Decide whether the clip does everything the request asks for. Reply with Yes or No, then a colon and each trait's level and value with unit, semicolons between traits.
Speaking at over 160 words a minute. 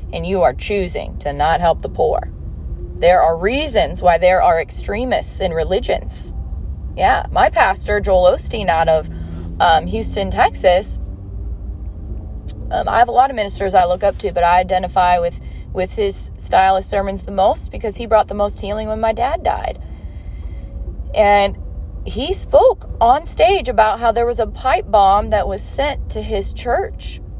Yes: average, 170 wpm